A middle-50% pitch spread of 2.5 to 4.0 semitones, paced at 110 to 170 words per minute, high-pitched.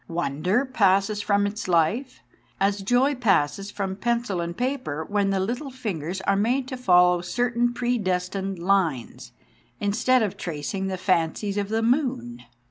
No: average, 5.1 semitones; average, 145 wpm; high, 200 Hz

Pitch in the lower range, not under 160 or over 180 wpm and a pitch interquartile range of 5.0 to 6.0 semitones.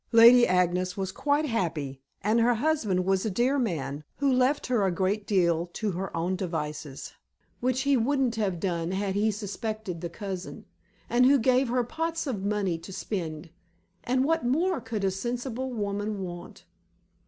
No: high, 210 Hz; average, 170 wpm; wide, 5.4 semitones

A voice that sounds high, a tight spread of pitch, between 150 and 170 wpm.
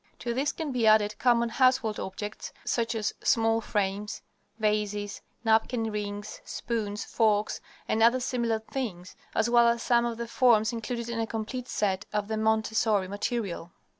Yes: high, 220 Hz; narrow, 2.1 semitones; average, 160 wpm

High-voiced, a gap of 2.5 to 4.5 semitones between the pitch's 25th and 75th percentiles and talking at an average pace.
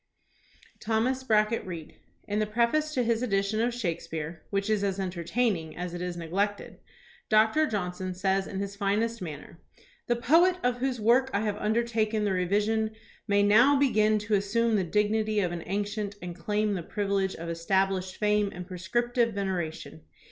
Yes: high, 205 Hz; average, 3.3 semitones; average, 170 wpm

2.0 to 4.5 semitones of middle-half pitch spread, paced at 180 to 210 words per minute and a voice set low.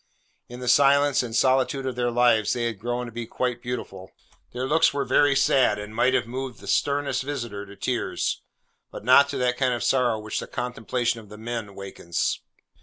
Yes: narrow, 2.4 semitones; average, 200 wpm; low, 125 Hz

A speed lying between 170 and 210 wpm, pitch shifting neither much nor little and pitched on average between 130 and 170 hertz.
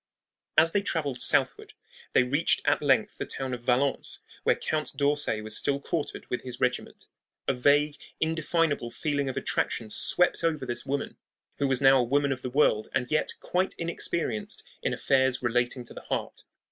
Yes: average, 175 wpm; average, 3.3 semitones; low, 135 Hz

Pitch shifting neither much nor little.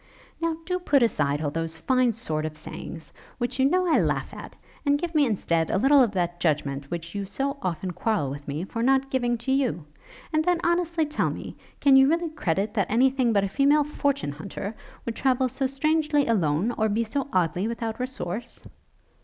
No: wide, 8.0 semitones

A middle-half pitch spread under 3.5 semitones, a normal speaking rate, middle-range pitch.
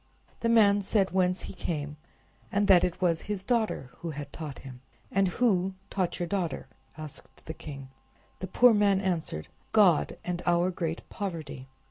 No: average, 4.0 semitones; average, 165 wpm; medium, 180 Hz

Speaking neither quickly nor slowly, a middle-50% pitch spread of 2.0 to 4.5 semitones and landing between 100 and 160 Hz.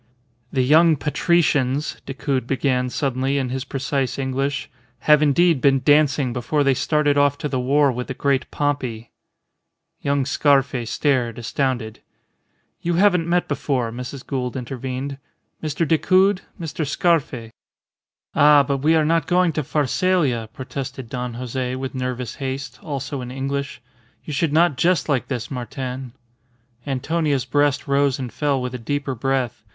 Yes: average, 145 wpm; average, 2.7 semitones; low, 135 Hz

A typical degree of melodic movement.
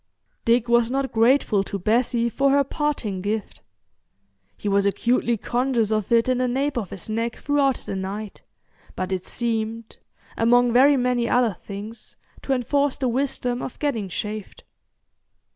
Yes: average, 3.1 semitones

